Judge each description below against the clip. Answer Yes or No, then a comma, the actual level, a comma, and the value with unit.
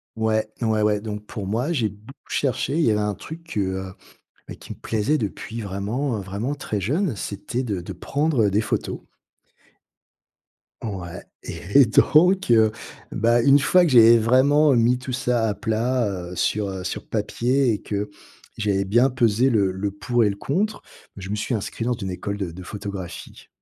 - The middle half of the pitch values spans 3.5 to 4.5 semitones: Yes, average, 4.0 semitones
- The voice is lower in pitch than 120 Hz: Yes, low, 110 Hz